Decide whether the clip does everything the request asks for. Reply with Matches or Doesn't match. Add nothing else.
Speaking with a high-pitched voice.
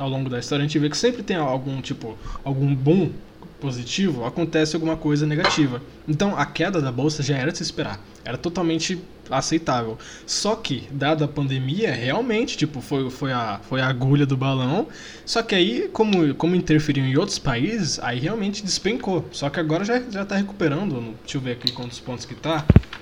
Doesn't match